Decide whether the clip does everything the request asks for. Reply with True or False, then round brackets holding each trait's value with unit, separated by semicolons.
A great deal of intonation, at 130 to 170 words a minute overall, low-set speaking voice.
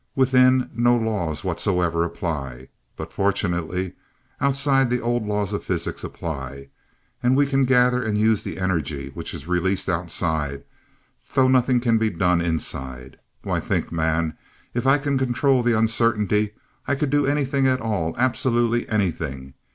True (7.2 semitones; 150 wpm; 105 Hz)